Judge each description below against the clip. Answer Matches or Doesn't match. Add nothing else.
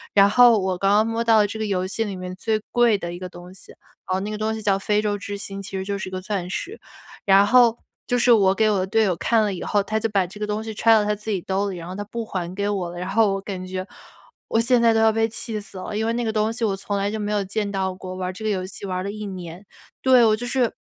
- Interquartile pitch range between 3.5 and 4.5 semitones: Doesn't match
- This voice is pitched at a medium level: Doesn't match